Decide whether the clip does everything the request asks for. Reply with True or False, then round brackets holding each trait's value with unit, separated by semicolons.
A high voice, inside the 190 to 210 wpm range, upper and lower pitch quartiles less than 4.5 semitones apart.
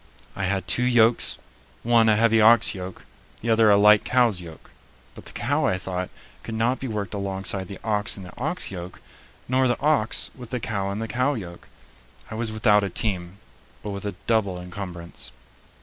False (105 Hz; 195 wpm; 3.3 semitones)